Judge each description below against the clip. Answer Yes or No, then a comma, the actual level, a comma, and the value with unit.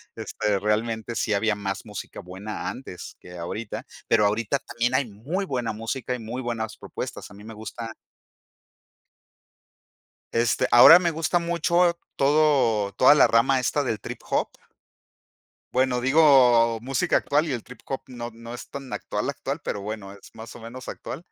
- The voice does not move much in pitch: No, average, 3.8 semitones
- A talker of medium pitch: No, low, 120 Hz